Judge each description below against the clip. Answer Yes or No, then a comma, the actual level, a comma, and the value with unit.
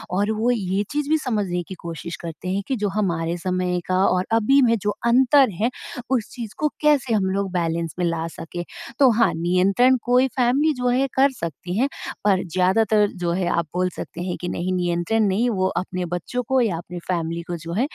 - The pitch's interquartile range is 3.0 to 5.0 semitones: No, wide, 5.6 semitones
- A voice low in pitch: No, high, 190 Hz